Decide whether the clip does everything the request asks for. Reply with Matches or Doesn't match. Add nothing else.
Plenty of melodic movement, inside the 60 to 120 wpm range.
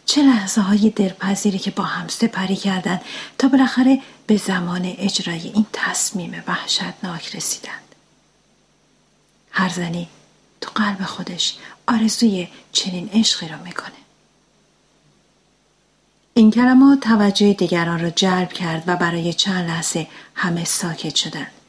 Doesn't match